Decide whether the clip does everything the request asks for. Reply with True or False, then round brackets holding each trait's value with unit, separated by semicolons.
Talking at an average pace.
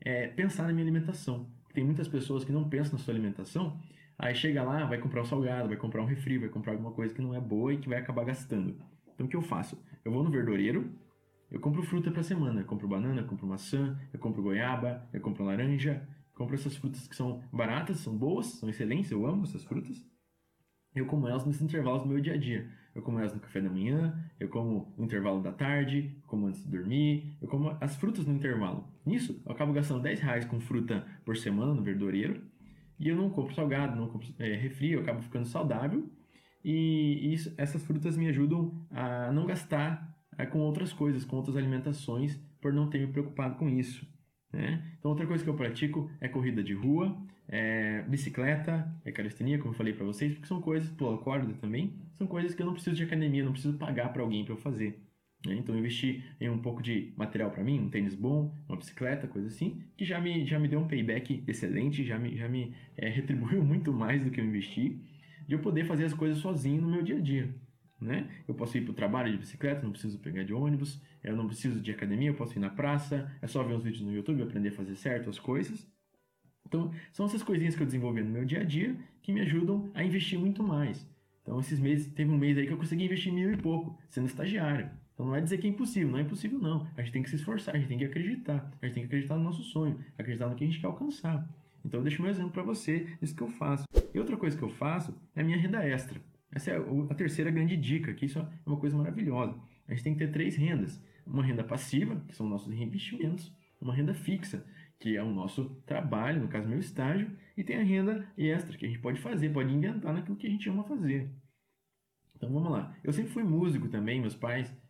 False (235 wpm)